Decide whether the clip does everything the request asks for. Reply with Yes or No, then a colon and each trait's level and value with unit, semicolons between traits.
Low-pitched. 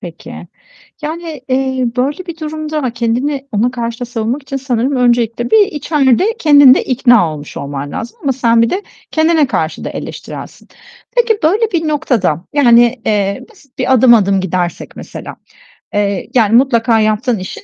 No: very high, 250 Hz